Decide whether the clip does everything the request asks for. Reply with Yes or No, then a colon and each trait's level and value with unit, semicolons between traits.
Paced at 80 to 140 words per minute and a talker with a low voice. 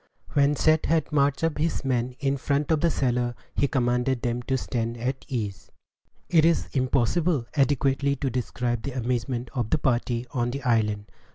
No: average, 175 wpm; low, 130 Hz